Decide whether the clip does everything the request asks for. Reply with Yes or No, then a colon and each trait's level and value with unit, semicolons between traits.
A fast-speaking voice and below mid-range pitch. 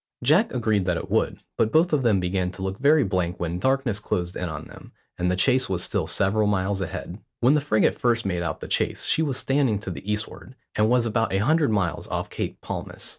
Yes: fast, 230 wpm; low, 105 Hz